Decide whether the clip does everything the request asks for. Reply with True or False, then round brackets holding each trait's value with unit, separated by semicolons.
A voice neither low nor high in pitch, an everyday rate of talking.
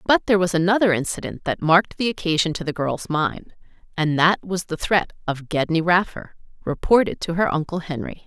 True (170 Hz; 190 wpm)